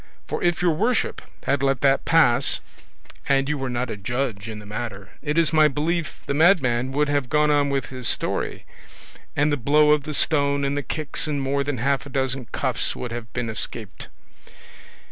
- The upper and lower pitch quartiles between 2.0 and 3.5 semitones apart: Yes, average, 3.2 semitones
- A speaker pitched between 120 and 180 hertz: Yes, medium, 140 Hz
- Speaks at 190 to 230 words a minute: Yes, average, 200 wpm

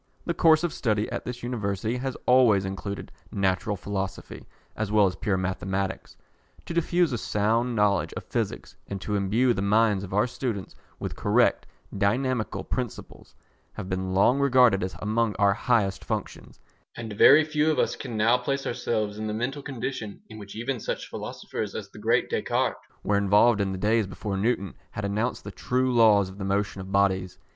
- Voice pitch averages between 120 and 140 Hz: No, low, 105 Hz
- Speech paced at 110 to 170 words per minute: No, average, 185 wpm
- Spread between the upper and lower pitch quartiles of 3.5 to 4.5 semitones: Yes, average, 3.9 semitones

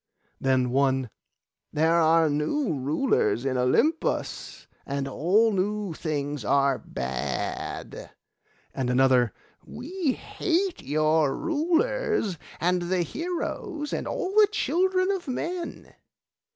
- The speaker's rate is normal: No, slow, 105 wpm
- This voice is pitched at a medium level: Yes, medium, 175 Hz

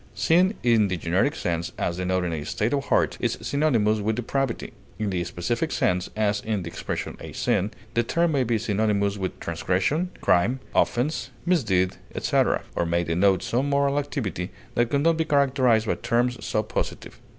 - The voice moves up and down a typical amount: No, wide, 6.9 semitones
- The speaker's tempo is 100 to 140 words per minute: No, average, 175 wpm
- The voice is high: No, low, 110 Hz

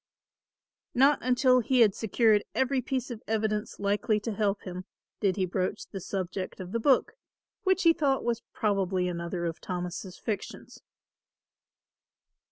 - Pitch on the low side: No, high, 210 Hz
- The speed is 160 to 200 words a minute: No, average, 145 wpm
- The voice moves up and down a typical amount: Yes, average, 4.8 semitones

